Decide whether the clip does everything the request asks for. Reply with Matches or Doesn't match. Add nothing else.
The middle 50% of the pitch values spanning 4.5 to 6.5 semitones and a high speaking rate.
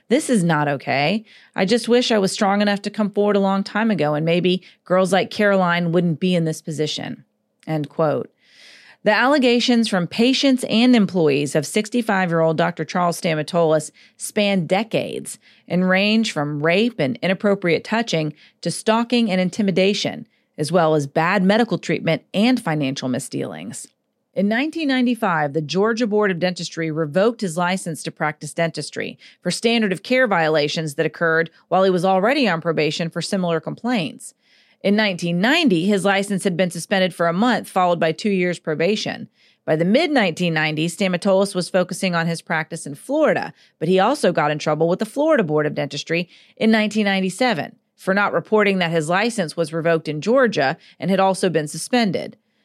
Doesn't match